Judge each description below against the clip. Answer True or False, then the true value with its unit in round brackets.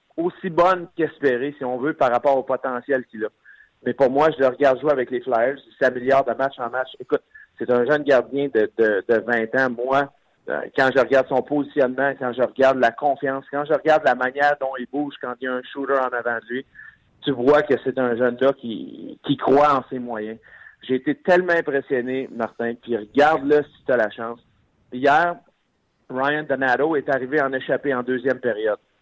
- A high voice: False (135 Hz)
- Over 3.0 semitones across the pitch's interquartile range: False (2.7 semitones)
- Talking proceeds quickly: False (210 wpm)